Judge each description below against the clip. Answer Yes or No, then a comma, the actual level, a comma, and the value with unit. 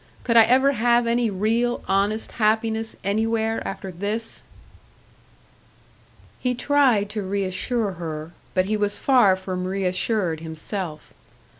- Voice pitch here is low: No, high, 210 Hz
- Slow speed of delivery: Yes, slow, 120 wpm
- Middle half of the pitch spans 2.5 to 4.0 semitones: Yes, average, 3.6 semitones